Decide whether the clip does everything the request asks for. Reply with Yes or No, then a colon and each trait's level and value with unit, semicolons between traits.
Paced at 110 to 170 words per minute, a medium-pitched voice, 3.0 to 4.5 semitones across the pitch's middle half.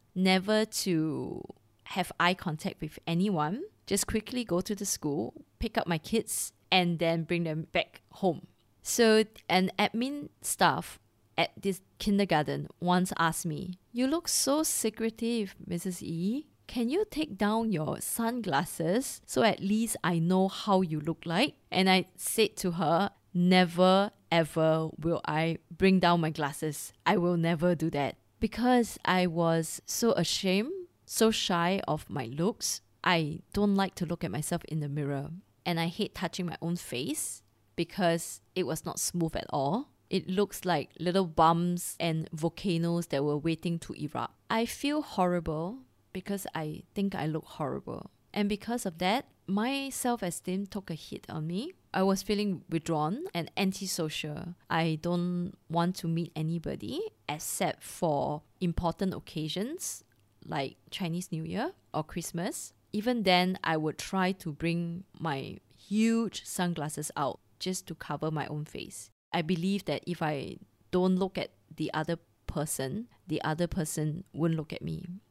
Yes: average, 155 wpm; medium, 175 Hz; average, 3.5 semitones